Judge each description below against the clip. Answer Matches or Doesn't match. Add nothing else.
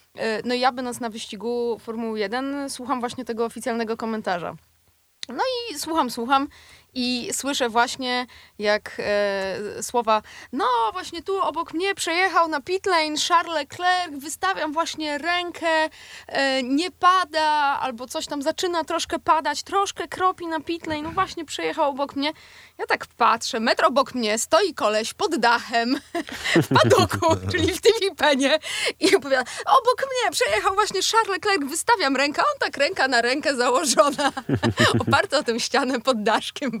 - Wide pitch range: Matches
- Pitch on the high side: Matches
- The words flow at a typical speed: Matches